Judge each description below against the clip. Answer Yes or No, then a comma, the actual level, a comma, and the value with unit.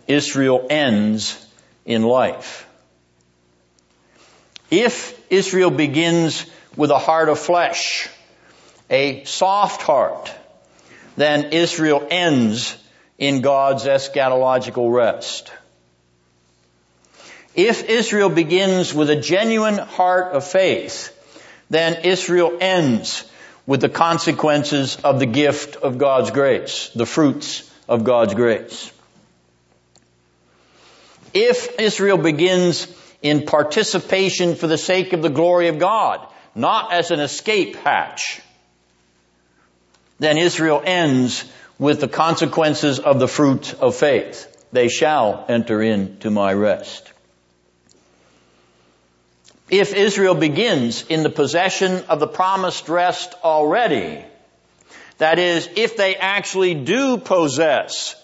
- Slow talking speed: Yes, slow, 105 wpm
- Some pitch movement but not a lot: No, wide, 8.1 semitones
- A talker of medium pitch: Yes, medium, 150 Hz